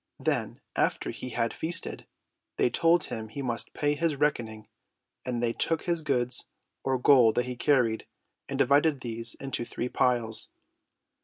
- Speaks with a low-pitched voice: Yes, low, 125 Hz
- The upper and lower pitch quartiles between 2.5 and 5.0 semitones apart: Yes, average, 3.8 semitones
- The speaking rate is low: No, average, 155 wpm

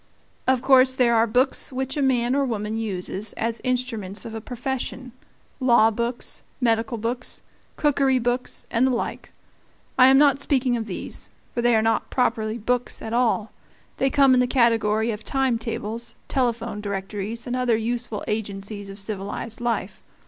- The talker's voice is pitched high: Yes, high, 235 Hz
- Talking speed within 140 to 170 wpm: Yes, average, 165 wpm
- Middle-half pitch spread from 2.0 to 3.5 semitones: Yes, narrow, 2.5 semitones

